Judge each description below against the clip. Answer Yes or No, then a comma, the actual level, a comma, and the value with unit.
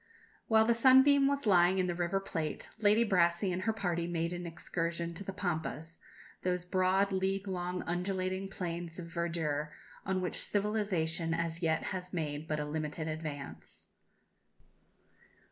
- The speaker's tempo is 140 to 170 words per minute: Yes, average, 150 wpm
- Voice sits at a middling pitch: Yes, medium, 175 Hz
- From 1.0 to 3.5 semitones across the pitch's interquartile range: Yes, average, 2.7 semitones